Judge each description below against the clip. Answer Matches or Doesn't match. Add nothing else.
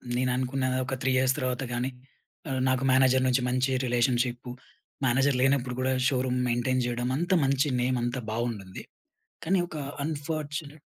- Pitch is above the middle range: Doesn't match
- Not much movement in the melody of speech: Matches